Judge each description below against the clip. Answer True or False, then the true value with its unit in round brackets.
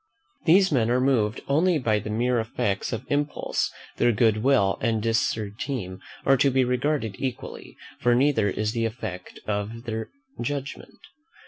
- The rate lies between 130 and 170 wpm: True (150 wpm)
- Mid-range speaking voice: False (115 Hz)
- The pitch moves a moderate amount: True (4.0 semitones)